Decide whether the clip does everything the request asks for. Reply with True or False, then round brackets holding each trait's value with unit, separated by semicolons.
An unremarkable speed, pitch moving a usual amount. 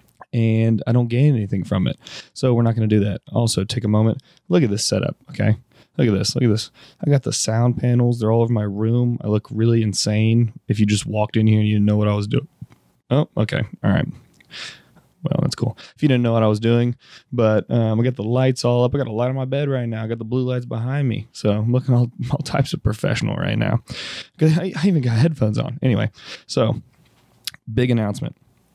False (240 wpm; 3.2 semitones)